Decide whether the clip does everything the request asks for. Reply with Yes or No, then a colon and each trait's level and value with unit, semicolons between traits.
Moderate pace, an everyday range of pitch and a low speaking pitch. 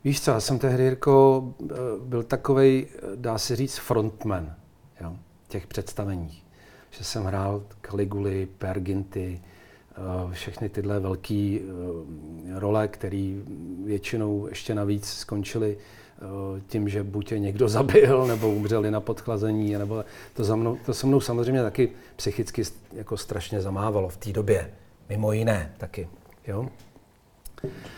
Yes: average, 125 wpm; average, 3.0 semitones; low, 105 Hz